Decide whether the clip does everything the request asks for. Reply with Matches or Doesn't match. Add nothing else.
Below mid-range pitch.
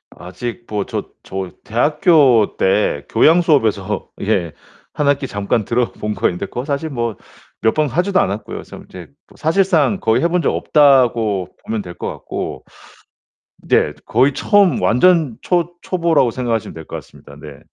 Matches